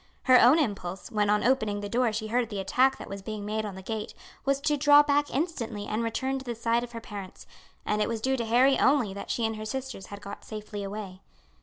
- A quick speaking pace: Yes, fast, 250 wpm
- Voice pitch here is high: Yes, high, 225 Hz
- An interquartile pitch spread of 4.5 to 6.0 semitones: No, average, 4.1 semitones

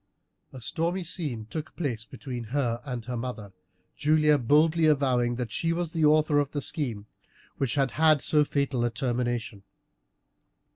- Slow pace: No, average, 155 wpm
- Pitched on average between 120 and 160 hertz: Yes, medium, 140 Hz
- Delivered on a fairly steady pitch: No, average, 4.2 semitones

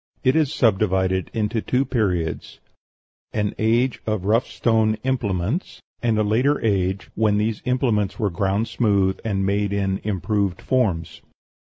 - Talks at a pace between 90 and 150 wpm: Yes, average, 140 wpm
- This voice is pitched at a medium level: No, low, 105 Hz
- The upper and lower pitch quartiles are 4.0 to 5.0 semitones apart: No, average, 3.1 semitones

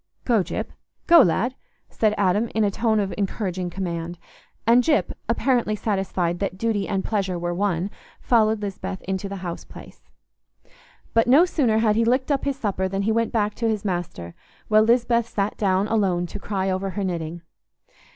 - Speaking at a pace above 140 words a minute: Yes, average, 180 wpm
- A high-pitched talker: Yes, high, 205 Hz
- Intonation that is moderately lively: Yes, average, 3.3 semitones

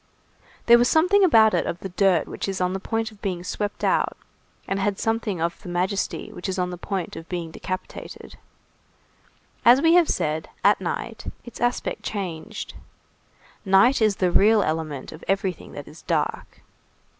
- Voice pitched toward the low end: No, high, 195 Hz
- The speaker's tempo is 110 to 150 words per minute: No, average, 170 wpm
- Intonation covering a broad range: No, average, 4.1 semitones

